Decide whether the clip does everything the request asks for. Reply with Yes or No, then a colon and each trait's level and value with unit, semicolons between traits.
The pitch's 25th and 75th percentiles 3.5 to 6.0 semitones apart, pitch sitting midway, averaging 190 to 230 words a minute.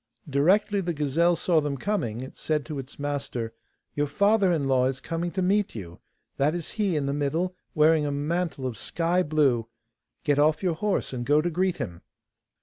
Yes: average, 4.2 semitones; medium, 150 Hz; average, 195 wpm